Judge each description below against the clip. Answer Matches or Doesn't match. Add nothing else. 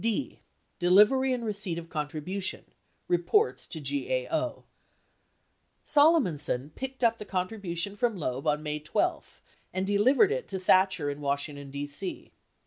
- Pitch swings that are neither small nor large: Doesn't match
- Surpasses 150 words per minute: Doesn't match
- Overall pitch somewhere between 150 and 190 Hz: Matches